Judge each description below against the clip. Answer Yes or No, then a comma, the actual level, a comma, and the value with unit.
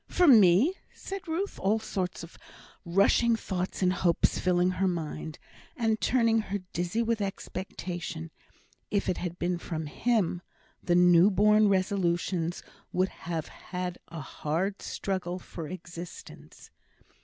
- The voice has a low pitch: No, medium, 185 Hz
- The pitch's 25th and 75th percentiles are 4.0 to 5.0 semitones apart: No, average, 3.3 semitones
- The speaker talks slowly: Yes, slow, 130 wpm